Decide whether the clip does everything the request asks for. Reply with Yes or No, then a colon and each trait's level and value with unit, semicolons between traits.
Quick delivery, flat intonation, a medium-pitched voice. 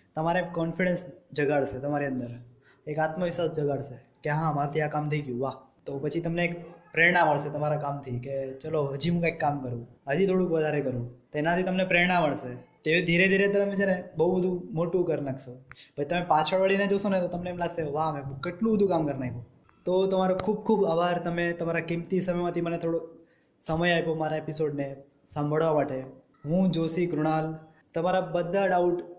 No: fast, 185 wpm; average, 3.4 semitones; medium, 165 Hz